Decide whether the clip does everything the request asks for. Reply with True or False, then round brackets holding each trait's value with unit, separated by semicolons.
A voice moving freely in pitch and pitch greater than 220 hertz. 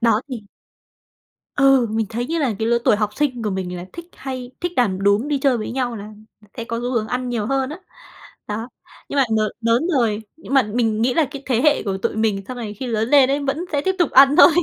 False (3.8 semitones; 245 Hz)